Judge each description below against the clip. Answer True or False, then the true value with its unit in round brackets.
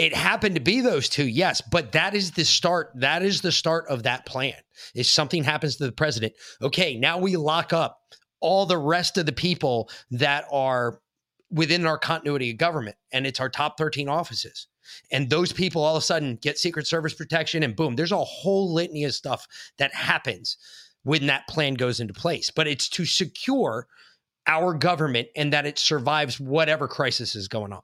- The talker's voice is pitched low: False (155 Hz)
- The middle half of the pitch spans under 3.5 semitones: False (3.9 semitones)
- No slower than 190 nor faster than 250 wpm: True (195 wpm)